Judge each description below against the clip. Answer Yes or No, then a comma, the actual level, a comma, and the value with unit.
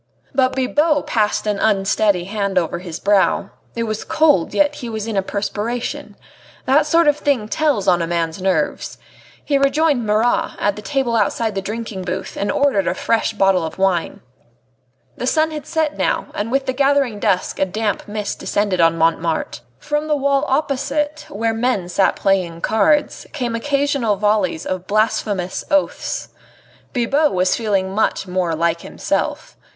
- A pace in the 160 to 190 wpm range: Yes, average, 165 wpm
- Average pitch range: No, wide, 6.4 semitones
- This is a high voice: Yes, high, 215 Hz